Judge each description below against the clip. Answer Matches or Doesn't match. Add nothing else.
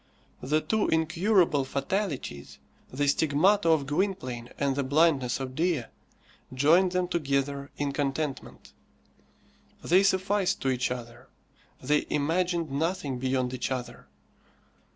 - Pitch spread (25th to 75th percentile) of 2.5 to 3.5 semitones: Doesn't match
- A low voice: Doesn't match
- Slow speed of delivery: Matches